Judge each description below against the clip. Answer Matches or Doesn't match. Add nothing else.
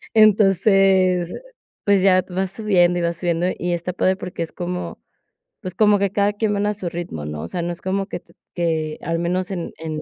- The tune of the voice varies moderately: Doesn't match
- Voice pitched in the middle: Matches